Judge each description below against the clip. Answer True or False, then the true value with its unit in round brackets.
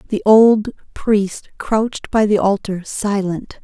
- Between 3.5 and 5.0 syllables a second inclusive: True (3.6 syllables/s)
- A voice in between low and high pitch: False (205 Hz)